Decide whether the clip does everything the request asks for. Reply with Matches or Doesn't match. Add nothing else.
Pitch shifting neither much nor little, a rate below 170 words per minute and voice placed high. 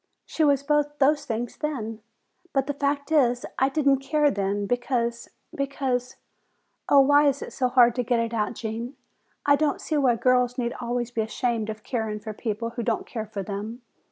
Doesn't match